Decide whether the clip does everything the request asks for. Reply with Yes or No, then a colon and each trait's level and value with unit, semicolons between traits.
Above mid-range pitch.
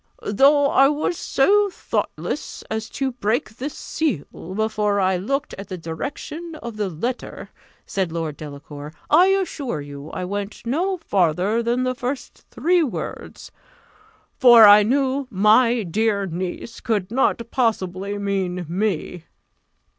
Yes: high, 220 Hz